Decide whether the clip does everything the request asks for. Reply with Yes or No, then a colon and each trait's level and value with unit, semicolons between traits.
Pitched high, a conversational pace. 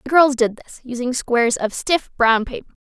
No: very high, 250 Hz; fast, 210 wpm